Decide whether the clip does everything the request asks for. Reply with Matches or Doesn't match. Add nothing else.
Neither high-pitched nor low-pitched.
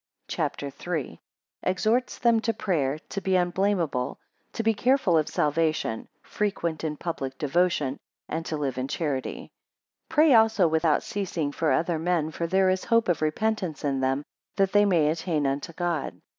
Matches